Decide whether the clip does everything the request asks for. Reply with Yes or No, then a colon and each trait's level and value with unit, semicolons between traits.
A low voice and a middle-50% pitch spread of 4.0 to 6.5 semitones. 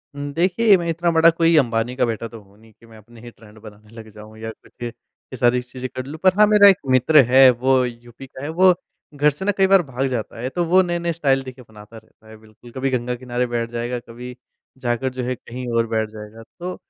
Yes: low, 125 Hz; average, 4.5 semitones